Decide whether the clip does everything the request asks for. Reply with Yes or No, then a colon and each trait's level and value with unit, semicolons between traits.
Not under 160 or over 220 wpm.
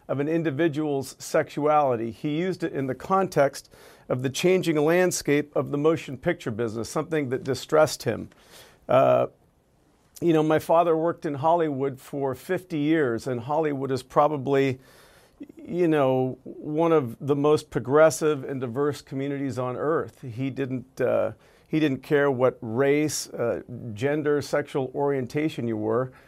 No: slow, 145 wpm